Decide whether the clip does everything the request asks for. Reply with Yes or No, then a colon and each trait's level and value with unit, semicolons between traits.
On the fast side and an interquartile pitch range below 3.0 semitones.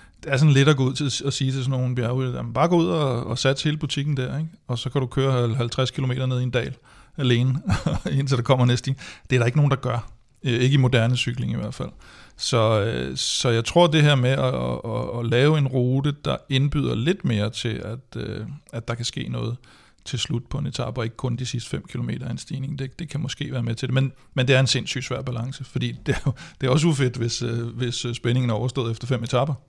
Yes: fast, 255 wpm; narrow, 2.5 semitones